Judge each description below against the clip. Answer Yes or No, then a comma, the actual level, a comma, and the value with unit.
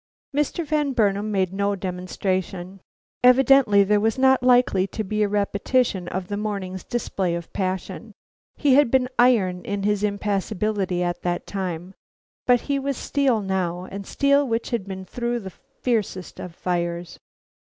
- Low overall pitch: No, high, 200 Hz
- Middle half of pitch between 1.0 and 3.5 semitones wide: No, average, 4.5 semitones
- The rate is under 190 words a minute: Yes, average, 155 wpm